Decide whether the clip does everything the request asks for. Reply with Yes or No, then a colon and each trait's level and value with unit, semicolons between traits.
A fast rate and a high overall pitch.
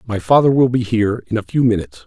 No: fast, 260 wpm; low, 115 Hz